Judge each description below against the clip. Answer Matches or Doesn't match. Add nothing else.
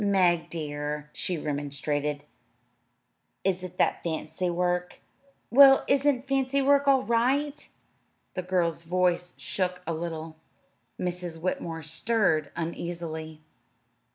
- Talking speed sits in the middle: Doesn't match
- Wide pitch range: Doesn't match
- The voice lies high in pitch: Doesn't match